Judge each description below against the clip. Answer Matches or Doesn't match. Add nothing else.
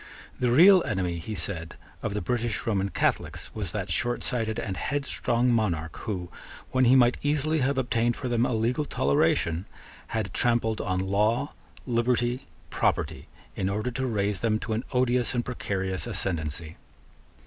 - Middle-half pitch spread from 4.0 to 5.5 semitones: Matches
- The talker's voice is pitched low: Matches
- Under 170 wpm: Matches